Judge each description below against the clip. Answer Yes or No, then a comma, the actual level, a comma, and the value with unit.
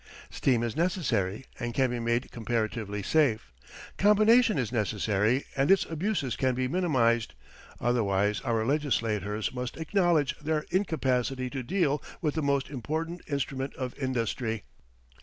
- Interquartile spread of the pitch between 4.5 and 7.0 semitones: Yes, average, 5.1 semitones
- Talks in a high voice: No, low, 130 Hz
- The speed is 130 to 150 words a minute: Yes, slow, 135 wpm